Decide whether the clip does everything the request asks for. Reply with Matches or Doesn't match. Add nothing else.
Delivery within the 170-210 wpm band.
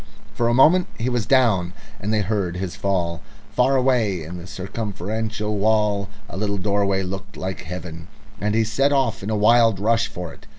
Matches